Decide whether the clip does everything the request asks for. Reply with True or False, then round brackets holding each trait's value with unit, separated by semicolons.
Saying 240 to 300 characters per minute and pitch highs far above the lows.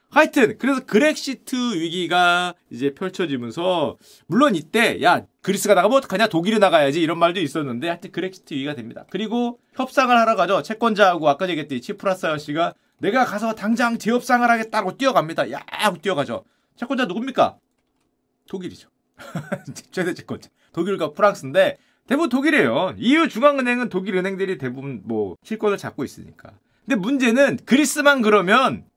False (390 characters per minute; 6.2 semitones)